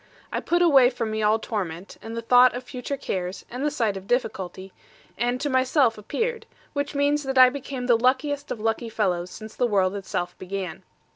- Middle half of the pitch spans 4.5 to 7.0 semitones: Yes, average, 4.9 semitones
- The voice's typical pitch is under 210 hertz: No, high, 240 Hz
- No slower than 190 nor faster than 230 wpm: Yes, average, 200 wpm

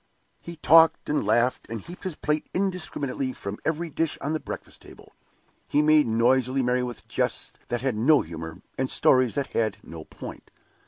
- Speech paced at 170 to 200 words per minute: Yes, average, 175 wpm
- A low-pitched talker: Yes, low, 130 Hz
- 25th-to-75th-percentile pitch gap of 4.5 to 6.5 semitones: Yes, average, 4.9 semitones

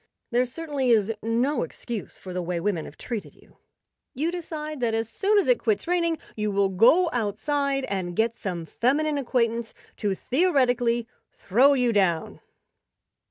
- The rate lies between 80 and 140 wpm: No, average, 160 wpm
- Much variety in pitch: Yes, wide, 5.8 semitones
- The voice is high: Yes, high, 240 Hz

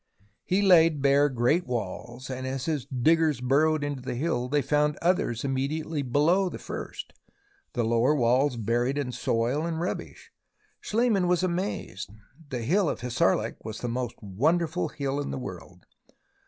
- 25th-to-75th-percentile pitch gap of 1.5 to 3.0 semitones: No, average, 4.8 semitones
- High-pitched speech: No, medium, 140 Hz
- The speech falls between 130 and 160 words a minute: Yes, average, 155 wpm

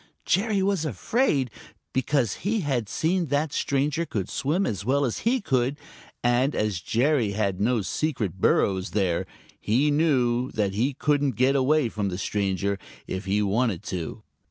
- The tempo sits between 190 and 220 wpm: No, average, 160 wpm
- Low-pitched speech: Yes, low, 125 Hz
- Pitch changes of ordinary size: No, wide, 6.4 semitones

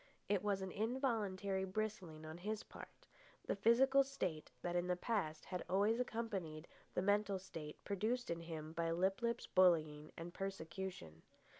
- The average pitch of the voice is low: No, high, 190 Hz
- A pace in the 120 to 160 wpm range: Yes, average, 155 wpm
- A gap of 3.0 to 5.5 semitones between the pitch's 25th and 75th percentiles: Yes, average, 4.4 semitones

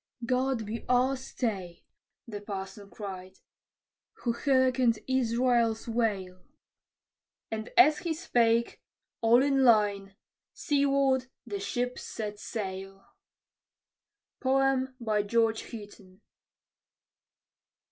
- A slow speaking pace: Yes, slow, 85 wpm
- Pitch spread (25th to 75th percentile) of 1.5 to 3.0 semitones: No, average, 4.1 semitones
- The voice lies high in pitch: Yes, high, 230 Hz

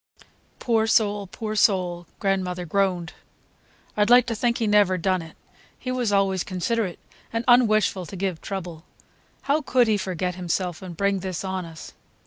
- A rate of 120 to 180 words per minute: Yes, average, 165 wpm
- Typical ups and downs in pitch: Yes, average, 3.3 semitones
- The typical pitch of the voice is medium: No, high, 195 Hz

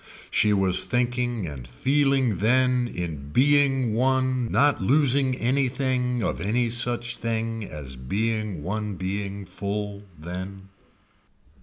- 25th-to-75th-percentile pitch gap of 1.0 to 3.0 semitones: No, average, 4.8 semitones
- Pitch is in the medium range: No, low, 115 Hz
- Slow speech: Yes, slow, 115 wpm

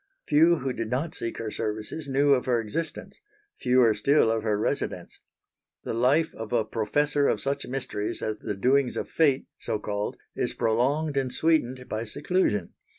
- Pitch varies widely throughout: No, average, 4.6 semitones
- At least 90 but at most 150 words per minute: No, average, 170 wpm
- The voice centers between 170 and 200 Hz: No, low, 125 Hz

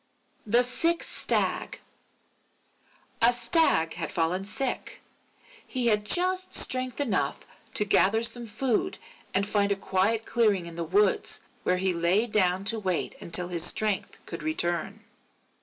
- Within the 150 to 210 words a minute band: No, average, 140 wpm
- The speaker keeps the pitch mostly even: No, average, 4.8 semitones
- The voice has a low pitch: No, high, 205 Hz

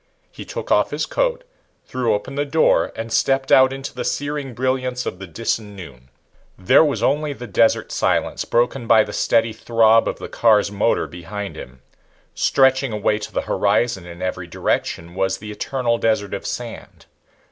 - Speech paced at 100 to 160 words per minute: No, average, 175 wpm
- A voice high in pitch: No, low, 115 Hz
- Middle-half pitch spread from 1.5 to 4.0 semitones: No, average, 4.6 semitones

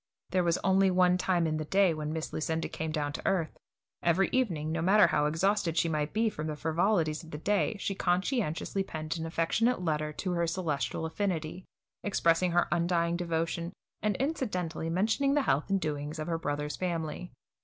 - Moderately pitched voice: Yes, medium, 170 Hz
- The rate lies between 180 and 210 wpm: Yes, average, 185 wpm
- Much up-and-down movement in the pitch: No, average, 3.3 semitones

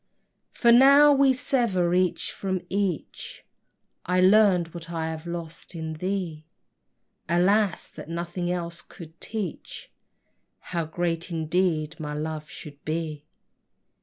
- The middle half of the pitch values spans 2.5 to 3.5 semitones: Yes, average, 2.9 semitones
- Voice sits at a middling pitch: Yes, medium, 175 Hz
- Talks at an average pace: No, slow, 120 wpm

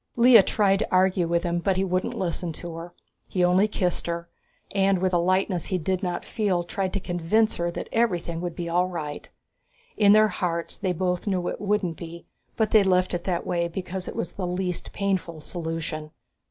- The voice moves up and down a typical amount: No, narrow, 2.2 semitones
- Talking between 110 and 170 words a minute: No, fast, 205 wpm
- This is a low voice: No, medium, 180 Hz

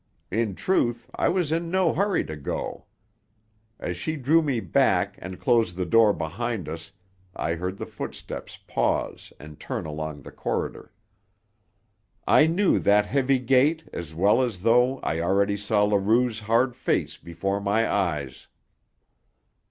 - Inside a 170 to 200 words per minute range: No, average, 145 wpm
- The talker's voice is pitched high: No, low, 105 Hz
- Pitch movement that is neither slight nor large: No, wide, 6.4 semitones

